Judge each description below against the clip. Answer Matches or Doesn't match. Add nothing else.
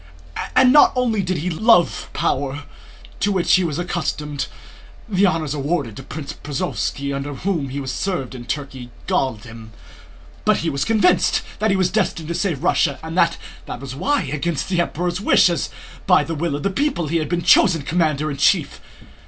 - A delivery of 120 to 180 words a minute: Doesn't match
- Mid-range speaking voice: Matches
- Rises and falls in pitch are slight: Doesn't match